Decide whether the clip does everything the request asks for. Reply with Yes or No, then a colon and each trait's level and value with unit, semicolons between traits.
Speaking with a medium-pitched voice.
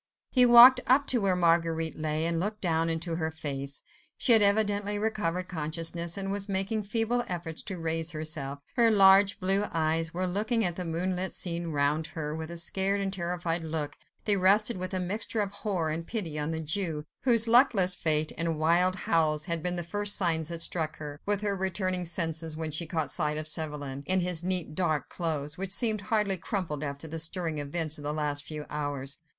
Yes: medium, 170 Hz